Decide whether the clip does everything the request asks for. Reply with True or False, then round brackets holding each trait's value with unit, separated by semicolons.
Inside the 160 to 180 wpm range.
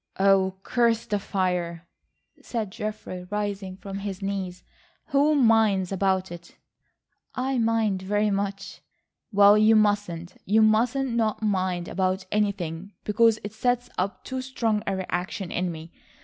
False (135 wpm)